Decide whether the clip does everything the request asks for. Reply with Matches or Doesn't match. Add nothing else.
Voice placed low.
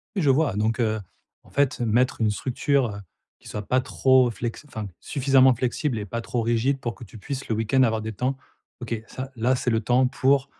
Matches